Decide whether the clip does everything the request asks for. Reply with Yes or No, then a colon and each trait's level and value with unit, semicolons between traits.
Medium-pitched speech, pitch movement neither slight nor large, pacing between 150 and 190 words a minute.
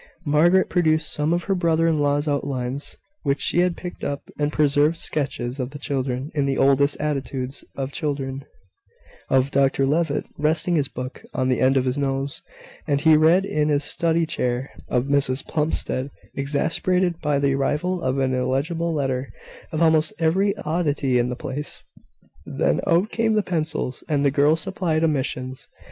Yes: medium, 145 Hz; average, 3.2 semitones; average, 170 wpm